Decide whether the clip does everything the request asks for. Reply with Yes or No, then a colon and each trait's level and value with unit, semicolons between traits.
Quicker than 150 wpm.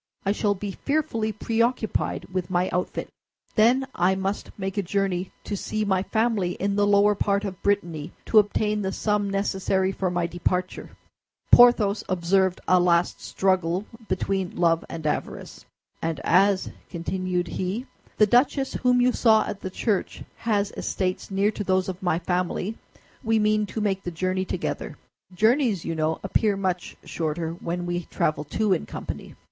Yes: average, 165 wpm